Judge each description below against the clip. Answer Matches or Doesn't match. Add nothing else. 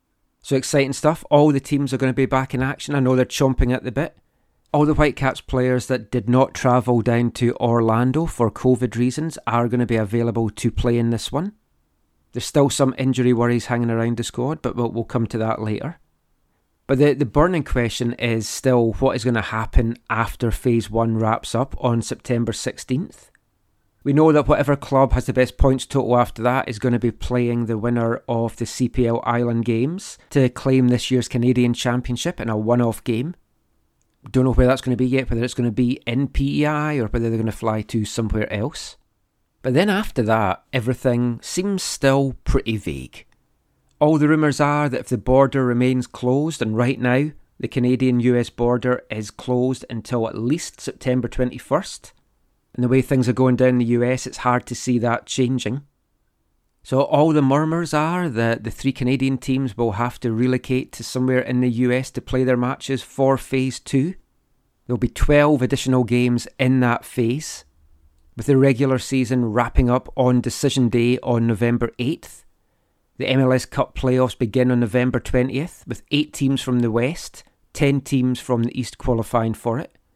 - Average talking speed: Matches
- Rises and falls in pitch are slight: Matches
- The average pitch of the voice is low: Matches